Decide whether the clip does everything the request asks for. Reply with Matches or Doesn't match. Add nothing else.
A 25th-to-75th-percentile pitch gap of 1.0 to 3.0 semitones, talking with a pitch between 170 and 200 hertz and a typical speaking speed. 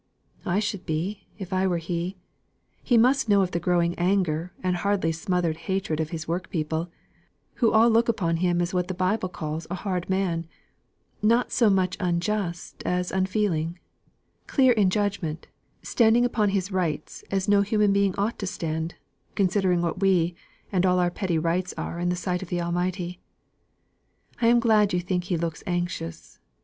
Matches